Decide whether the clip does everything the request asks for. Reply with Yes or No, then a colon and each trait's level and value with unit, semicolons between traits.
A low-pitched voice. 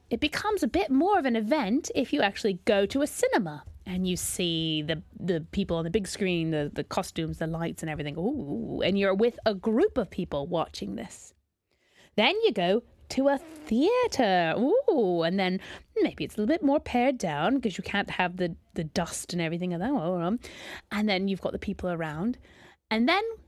No: high, 205 Hz